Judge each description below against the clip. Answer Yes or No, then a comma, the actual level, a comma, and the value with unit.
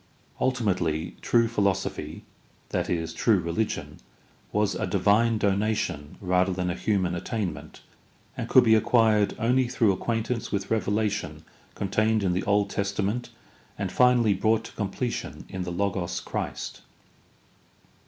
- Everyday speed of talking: No, slow, 125 wpm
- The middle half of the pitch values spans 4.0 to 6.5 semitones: No, average, 3.3 semitones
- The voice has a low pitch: Yes, low, 100 Hz